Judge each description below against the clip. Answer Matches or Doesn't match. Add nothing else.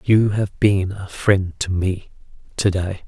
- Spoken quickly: Doesn't match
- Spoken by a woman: Doesn't match